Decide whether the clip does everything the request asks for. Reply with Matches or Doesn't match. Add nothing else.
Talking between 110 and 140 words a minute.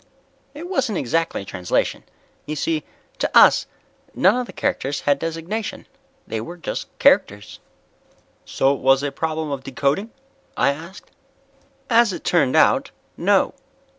Matches